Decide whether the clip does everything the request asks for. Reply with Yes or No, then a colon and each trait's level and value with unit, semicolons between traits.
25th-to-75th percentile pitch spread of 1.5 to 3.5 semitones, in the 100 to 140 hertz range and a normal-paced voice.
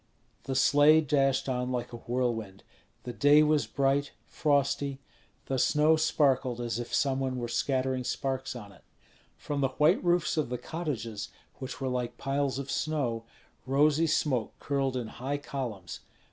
Yes: average, 2.7 semitones; low, 135 Hz; average, 160 wpm